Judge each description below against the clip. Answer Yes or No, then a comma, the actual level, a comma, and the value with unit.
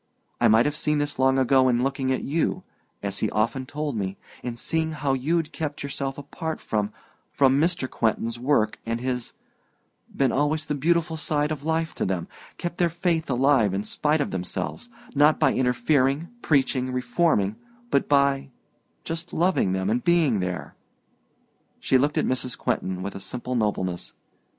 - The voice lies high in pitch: No, low, 135 Hz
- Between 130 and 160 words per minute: No, average, 170 wpm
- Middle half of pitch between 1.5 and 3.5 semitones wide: No, average, 4.6 semitones